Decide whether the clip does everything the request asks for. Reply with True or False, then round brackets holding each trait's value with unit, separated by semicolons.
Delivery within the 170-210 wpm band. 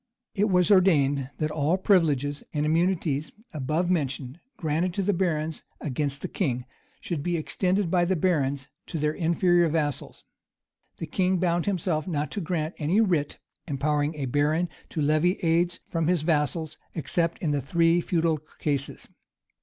False (160 wpm)